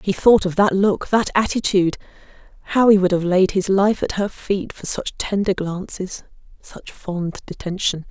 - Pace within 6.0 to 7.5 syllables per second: No, 4.6 syllables/s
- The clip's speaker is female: Yes, female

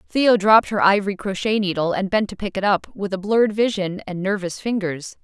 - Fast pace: Yes, fast, 220 wpm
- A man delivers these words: No, female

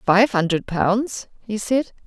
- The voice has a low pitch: No, high, 210 Hz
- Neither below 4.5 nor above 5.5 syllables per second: No, 3.5 syllables/s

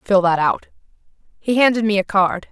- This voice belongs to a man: No, female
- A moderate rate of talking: Yes, average, 190 wpm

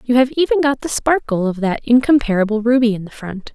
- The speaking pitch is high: Yes, high, 235 Hz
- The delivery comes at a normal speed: No, fast, 220 wpm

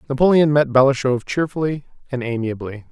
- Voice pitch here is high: No, low, 135 Hz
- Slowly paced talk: Yes, slow, 125 wpm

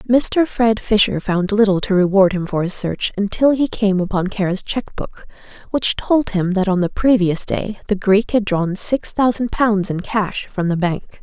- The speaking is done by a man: No, female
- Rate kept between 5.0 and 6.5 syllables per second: No, 4.6 syllables/s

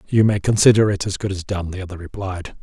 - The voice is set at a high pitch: No, very low, 95 Hz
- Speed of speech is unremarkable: No, fast, 250 wpm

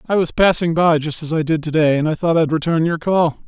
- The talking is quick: Yes, fast, 295 wpm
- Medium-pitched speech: Yes, medium, 160 Hz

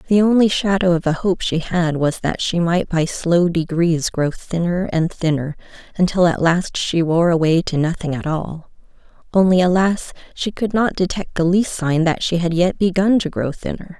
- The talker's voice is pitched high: No, medium, 175 Hz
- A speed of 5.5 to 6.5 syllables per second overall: No, 4.7 syllables/s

